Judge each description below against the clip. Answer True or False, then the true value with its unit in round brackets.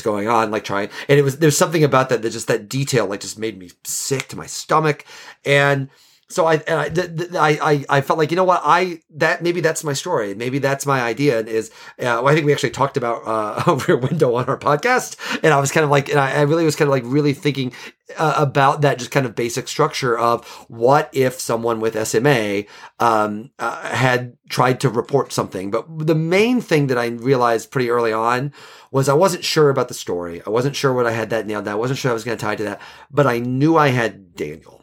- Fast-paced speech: True (245 wpm)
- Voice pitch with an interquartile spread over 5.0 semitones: False (4.4 semitones)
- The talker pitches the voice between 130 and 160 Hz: True (135 Hz)